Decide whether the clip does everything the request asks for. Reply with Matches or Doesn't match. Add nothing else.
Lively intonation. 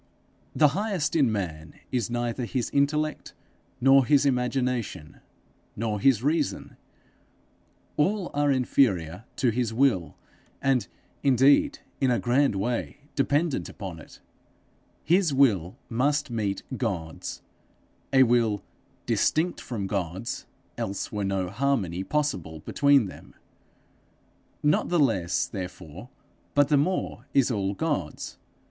Matches